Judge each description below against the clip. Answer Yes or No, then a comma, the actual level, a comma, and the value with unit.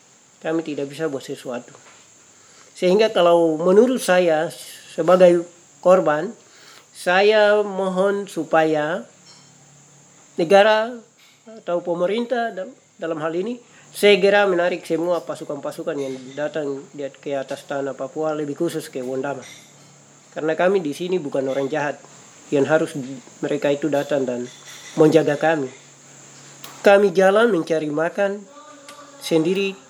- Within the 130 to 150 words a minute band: No, average, 110 wpm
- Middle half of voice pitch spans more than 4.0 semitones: Yes, average, 4.9 semitones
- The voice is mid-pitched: Yes, medium, 165 Hz